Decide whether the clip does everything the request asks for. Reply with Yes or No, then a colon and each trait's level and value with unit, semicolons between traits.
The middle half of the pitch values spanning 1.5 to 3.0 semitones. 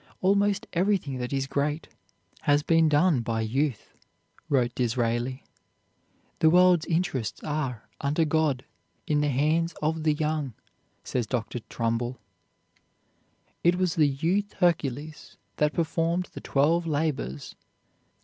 No: average, 4.2 semitones